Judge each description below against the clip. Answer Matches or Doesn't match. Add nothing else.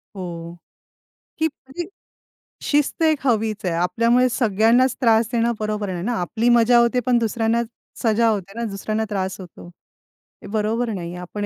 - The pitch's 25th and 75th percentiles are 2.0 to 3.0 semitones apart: Doesn't match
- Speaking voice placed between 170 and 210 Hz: Doesn't match